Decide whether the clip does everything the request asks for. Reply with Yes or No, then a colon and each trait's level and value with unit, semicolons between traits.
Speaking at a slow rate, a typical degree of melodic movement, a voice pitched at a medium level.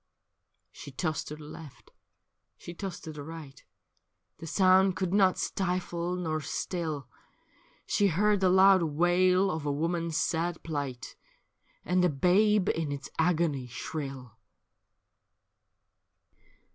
Yes: slow, 120 wpm; average, 3.5 semitones; medium, 170 Hz